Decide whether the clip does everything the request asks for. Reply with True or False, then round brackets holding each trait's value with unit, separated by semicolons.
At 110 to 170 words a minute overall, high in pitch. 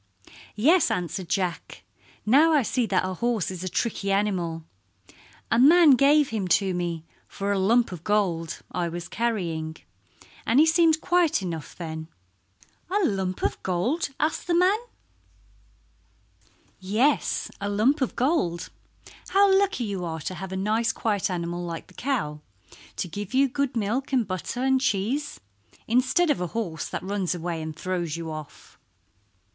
True (160 wpm; 205 Hz)